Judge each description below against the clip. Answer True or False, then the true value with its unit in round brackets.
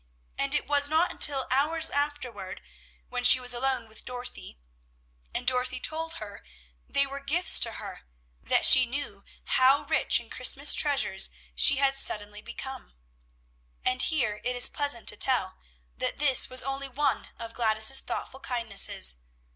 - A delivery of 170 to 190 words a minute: False (155 wpm)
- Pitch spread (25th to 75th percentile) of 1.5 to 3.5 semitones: True (3.1 semitones)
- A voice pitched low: False (260 Hz)